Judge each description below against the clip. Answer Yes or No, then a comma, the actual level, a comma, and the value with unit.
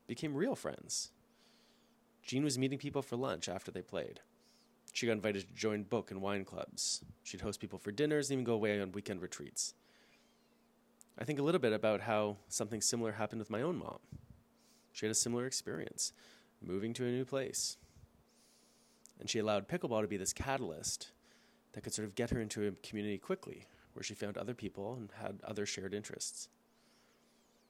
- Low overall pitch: Yes, low, 110 Hz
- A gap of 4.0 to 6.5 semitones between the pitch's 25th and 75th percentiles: Yes, average, 4.9 semitones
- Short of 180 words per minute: No, average, 185 wpm